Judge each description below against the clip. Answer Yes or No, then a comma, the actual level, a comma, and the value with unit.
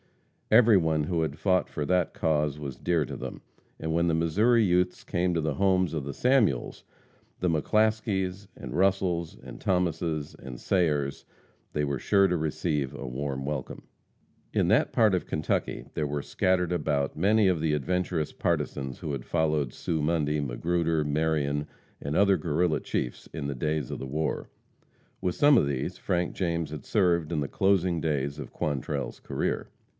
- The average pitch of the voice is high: No, very low, 80 Hz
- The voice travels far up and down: No, average, 3.7 semitones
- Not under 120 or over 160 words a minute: No, average, 170 wpm